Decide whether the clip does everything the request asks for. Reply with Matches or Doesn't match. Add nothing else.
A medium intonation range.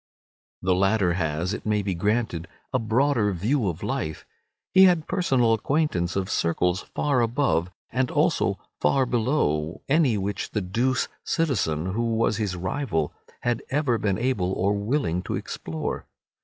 Doesn't match